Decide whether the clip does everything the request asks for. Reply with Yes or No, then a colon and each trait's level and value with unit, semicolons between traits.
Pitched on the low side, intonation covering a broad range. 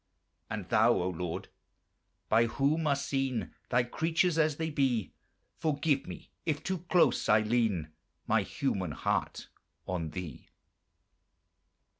Yes: low, 120 Hz; wide, 7.3 semitones